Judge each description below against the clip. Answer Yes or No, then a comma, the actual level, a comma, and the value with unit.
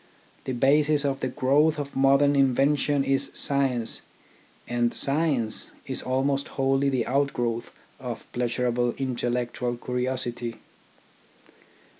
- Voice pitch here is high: No, low, 135 Hz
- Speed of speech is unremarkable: No, slow, 110 wpm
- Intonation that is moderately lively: No, narrow, 2.3 semitones